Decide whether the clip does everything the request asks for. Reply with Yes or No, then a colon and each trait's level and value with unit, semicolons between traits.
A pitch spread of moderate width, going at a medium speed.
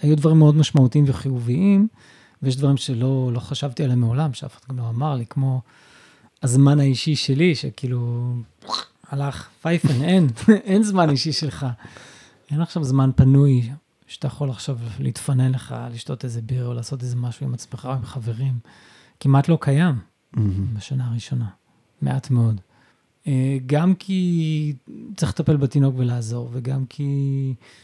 Yes: average, 3.1 semitones; average, 140 wpm